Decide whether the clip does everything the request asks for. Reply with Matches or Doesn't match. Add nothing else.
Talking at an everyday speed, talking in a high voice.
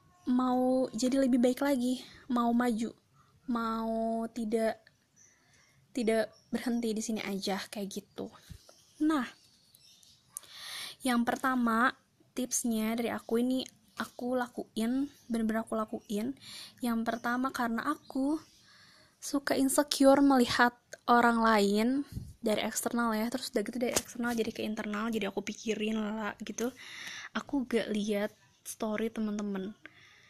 Matches